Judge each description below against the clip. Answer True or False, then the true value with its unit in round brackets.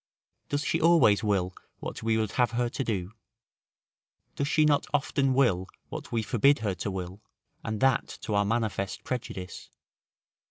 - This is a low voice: True (115 Hz)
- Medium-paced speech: True (160 wpm)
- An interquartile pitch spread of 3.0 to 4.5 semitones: False (5.0 semitones)